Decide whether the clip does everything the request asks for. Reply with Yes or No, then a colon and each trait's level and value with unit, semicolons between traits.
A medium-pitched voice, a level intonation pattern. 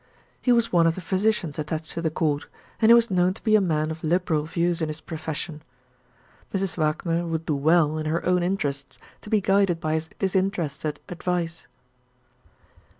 No: medium, 170 Hz; average, 3.1 semitones